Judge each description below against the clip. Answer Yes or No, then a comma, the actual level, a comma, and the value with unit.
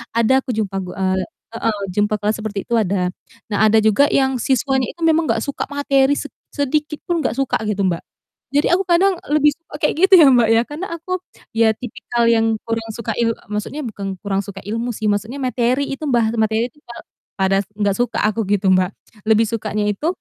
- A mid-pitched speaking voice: No, high, 230 Hz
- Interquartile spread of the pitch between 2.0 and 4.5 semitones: No, average, 5.2 semitones